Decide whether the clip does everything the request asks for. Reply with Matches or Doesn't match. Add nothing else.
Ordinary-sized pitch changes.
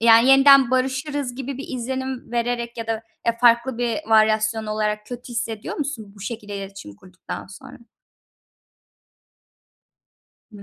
Matches